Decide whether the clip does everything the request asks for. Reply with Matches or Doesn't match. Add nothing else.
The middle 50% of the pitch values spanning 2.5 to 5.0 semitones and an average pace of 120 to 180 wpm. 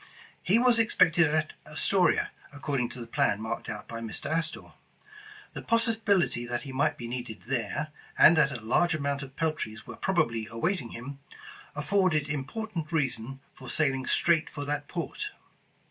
Doesn't match